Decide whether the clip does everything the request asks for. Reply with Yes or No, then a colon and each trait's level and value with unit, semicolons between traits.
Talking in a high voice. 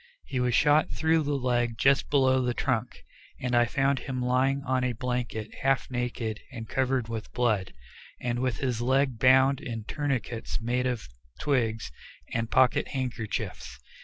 No: low, 125 Hz